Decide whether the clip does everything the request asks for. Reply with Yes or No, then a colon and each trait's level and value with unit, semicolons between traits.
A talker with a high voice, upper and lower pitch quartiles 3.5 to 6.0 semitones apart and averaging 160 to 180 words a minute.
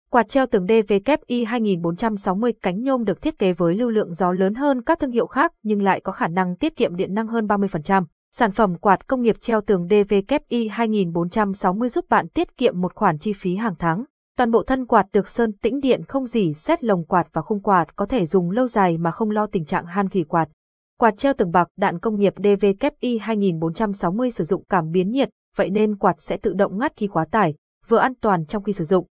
No: high, 210 Hz; average, 3.9 semitones; average, 225 wpm